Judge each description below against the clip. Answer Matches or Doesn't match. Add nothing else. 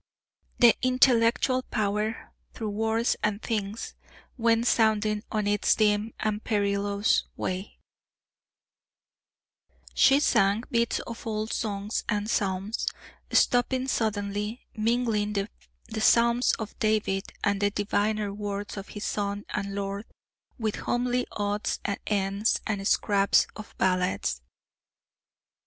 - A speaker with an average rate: Doesn't match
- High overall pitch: Matches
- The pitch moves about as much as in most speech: Doesn't match